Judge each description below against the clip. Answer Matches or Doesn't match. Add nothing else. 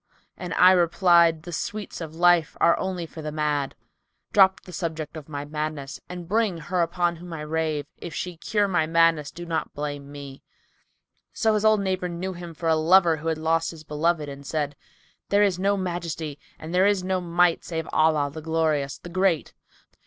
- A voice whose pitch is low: Doesn't match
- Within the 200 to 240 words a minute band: Matches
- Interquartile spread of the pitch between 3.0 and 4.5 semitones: Doesn't match